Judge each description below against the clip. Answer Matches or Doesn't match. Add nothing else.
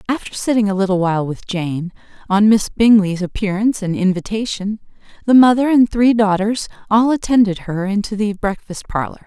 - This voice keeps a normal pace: Matches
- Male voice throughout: Doesn't match